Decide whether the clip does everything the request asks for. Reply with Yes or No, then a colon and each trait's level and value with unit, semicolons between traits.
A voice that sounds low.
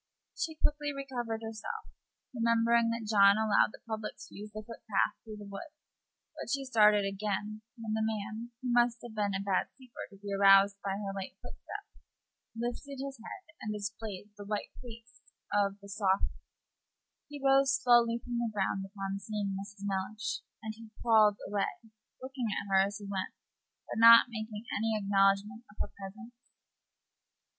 No: high, 215 Hz